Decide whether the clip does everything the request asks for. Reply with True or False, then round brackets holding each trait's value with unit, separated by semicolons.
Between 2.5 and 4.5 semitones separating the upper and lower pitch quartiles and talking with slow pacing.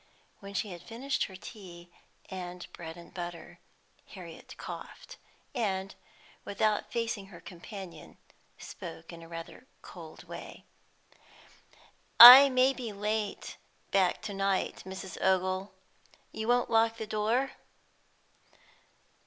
True (4.0 semitones; 115 wpm)